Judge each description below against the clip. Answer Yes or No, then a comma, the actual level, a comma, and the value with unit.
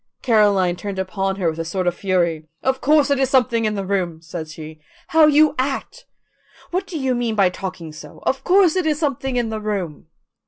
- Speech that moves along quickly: Yes, fast, 210 wpm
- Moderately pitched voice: No, high, 210 Hz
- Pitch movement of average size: No, wide, 7.0 semitones